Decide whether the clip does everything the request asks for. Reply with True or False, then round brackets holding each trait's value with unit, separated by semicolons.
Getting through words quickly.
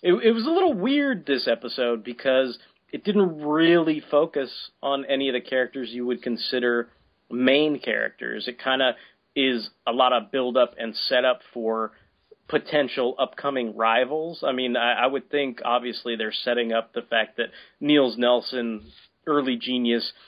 False (160 wpm)